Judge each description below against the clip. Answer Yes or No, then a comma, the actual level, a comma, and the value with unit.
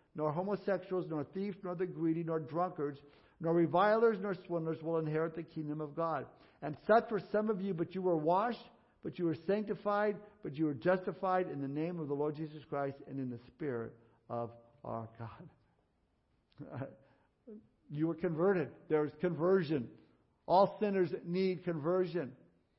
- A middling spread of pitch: Yes, average, 3.9 semitones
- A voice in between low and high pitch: Yes, medium, 170 Hz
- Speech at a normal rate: Yes, average, 165 wpm